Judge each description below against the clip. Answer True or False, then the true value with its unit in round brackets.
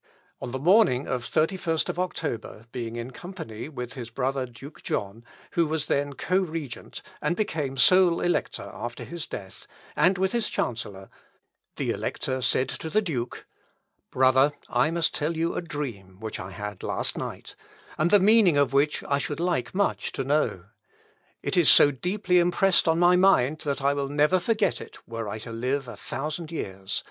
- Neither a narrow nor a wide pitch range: False (5.9 semitones)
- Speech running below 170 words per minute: False (180 wpm)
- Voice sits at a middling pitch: True (145 Hz)